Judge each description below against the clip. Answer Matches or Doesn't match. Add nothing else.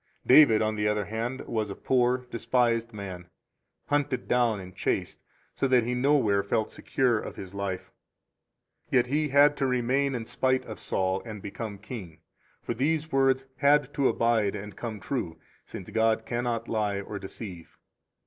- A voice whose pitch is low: Matches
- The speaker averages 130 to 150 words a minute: Doesn't match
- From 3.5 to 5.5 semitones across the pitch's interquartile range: Matches